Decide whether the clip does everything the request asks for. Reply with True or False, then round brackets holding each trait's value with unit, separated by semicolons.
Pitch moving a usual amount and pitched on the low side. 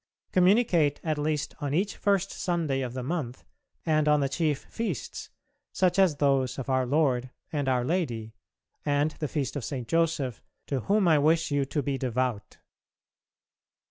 False (4.0 semitones; 145 Hz)